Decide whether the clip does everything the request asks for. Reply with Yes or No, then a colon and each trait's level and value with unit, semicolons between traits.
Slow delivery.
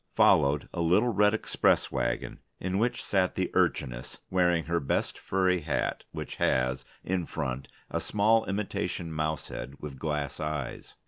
No: average, 150 wpm